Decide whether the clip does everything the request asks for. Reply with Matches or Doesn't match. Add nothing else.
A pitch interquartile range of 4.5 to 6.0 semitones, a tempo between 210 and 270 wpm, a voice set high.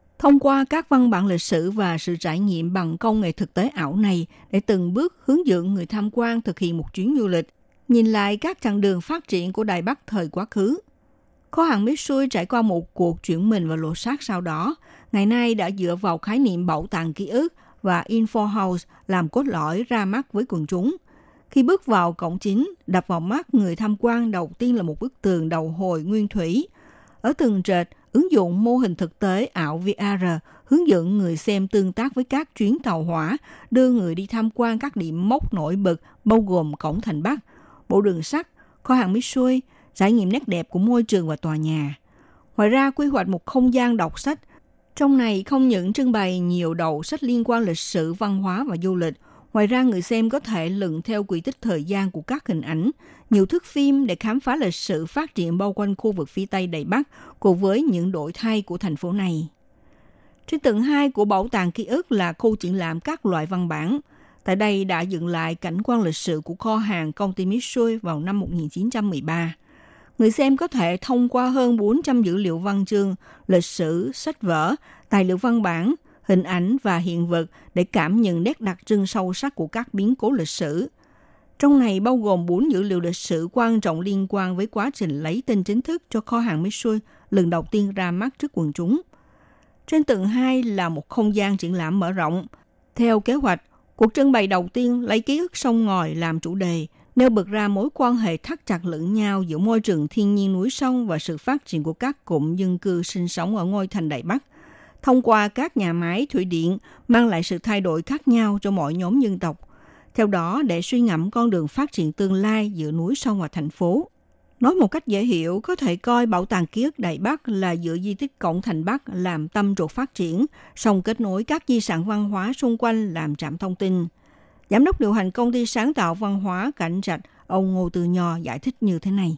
Matches